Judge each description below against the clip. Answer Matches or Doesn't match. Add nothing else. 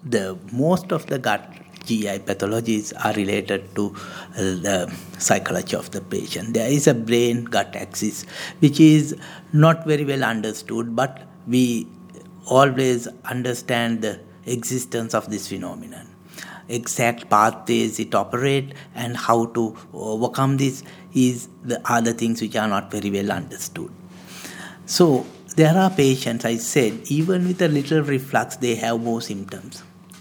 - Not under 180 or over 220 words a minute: Doesn't match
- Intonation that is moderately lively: Matches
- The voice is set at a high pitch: Doesn't match